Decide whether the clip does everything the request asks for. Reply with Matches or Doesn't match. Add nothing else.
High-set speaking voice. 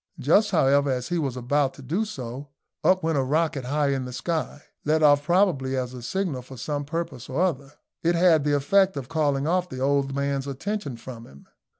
Doesn't match